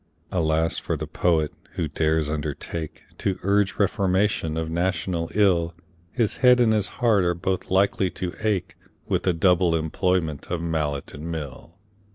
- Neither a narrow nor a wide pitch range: Yes, average, 3.2 semitones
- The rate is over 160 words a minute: No, average, 155 wpm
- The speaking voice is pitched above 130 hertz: No, very low, 85 Hz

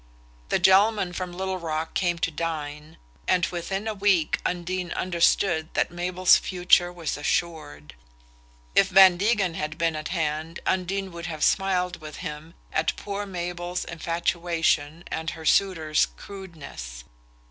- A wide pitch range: No, narrow, 2.6 semitones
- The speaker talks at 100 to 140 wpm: Yes, slow, 135 wpm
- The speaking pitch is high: No, medium, 175 Hz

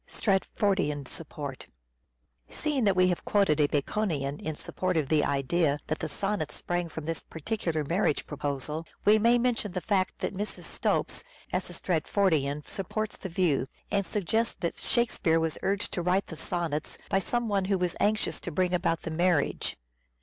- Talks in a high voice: No, medium, 175 Hz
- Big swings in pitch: No, average, 4.3 semitones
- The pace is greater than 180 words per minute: No, average, 170 wpm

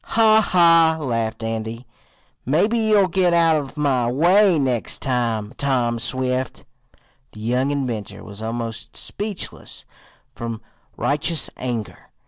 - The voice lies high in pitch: No, low, 130 Hz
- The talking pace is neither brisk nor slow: No, slow, 115 wpm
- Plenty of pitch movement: Yes, wide, 6.3 semitones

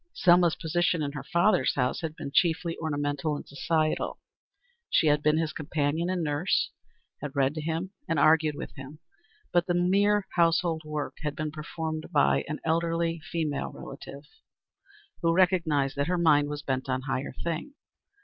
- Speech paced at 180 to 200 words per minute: No, average, 165 wpm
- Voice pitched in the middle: Yes, medium, 155 Hz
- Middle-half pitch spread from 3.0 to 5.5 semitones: No, narrow, 2.6 semitones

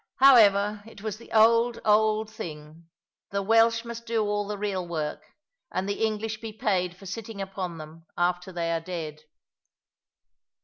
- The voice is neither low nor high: No, high, 205 Hz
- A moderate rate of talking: Yes, average, 160 wpm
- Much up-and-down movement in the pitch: No, average, 3.9 semitones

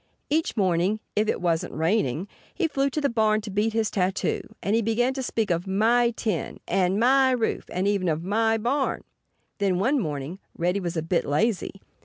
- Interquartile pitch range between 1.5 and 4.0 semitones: No, average, 4.4 semitones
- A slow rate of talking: No, average, 190 wpm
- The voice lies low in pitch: No, high, 210 Hz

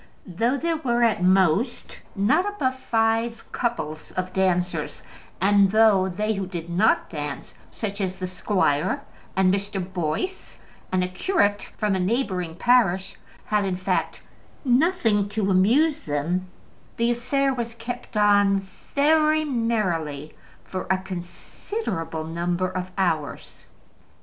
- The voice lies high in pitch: Yes, high, 195 Hz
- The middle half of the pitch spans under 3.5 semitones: No, average, 4.6 semitones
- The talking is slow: Yes, slow, 130 wpm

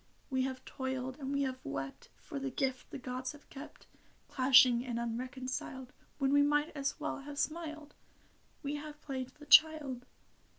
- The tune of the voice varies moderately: No, narrow, 2.3 semitones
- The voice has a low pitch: No, very high, 270 Hz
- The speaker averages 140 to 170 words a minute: Yes, average, 165 wpm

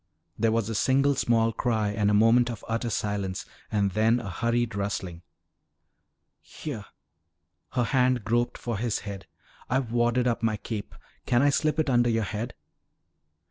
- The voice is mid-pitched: No, low, 115 Hz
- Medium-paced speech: Yes, average, 160 wpm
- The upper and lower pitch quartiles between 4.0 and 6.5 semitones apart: No, narrow, 2.6 semitones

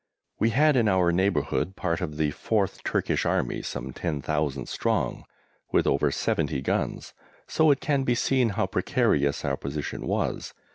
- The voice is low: Yes, very low, 90 Hz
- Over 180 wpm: No, average, 155 wpm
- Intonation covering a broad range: Yes, wide, 7.9 semitones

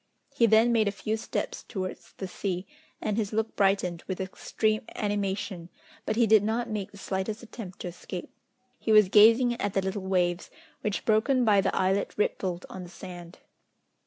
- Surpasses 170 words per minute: Yes, average, 180 wpm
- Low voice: No, high, 200 Hz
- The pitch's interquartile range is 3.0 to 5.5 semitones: No, narrow, 2.6 semitones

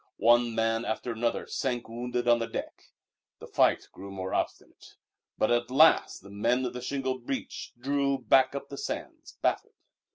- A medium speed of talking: Yes, average, 165 wpm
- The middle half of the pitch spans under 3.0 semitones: Yes, narrow, 2.4 semitones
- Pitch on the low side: Yes, low, 120 Hz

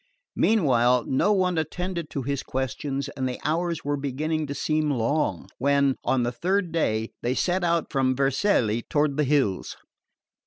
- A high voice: No, medium, 140 Hz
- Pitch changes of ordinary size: Yes, average, 3.9 semitones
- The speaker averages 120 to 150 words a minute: No, average, 160 wpm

